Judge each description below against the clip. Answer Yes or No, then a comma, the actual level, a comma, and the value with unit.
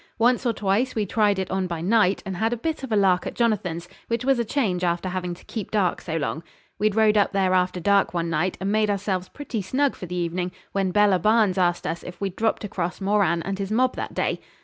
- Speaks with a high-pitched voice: Yes, high, 195 Hz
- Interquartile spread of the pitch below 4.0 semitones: Yes, average, 3.3 semitones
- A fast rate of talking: Yes, fast, 245 wpm